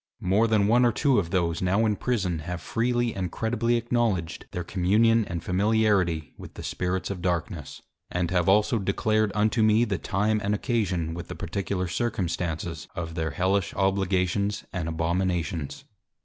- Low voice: Yes, very low, 95 Hz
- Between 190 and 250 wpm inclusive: No, average, 165 wpm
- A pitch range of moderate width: Yes, average, 3.8 semitones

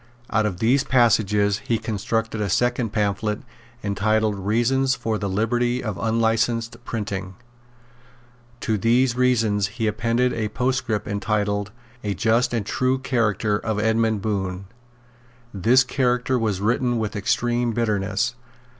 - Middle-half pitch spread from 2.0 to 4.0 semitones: Yes, average, 2.7 semitones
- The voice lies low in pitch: Yes, low, 110 Hz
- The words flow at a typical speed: No, slow, 130 wpm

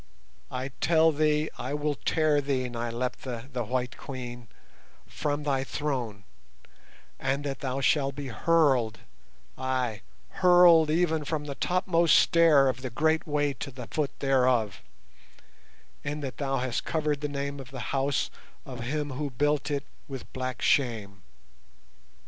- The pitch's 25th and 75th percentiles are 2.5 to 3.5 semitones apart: Yes, average, 2.8 semitones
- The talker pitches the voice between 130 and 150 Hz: Yes, medium, 140 Hz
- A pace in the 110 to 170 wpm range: Yes, average, 140 wpm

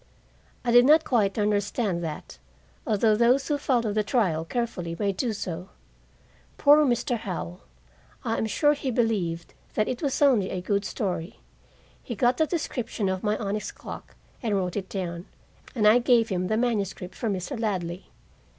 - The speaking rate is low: No, average, 170 wpm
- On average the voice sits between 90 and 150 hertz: No, high, 215 Hz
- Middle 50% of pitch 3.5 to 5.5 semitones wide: Yes, average, 4.3 semitones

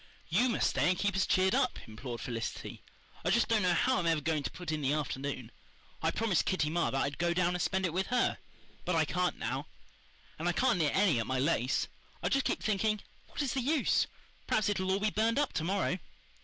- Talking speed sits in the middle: No, fast, 235 wpm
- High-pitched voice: No, medium, 180 Hz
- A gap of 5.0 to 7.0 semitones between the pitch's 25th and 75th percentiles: Yes, wide, 5.5 semitones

